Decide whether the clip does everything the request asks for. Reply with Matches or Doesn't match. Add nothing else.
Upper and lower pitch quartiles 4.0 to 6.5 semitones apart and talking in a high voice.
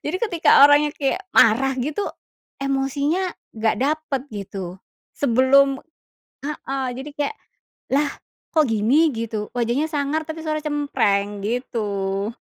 Matches